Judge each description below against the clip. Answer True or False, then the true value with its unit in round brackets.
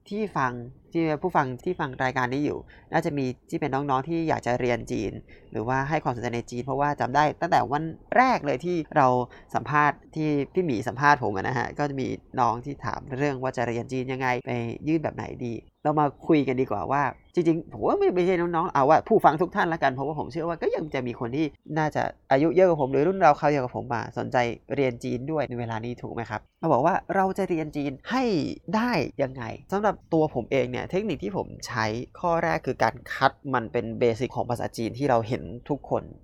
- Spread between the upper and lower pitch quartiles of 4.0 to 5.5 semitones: True (4.5 semitones)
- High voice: False (135 Hz)